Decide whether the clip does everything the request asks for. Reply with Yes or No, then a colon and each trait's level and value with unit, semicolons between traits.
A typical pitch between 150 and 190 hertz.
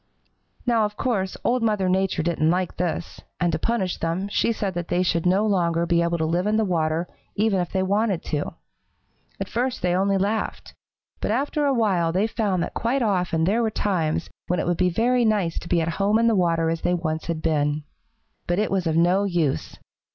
Yes: medium, 185 Hz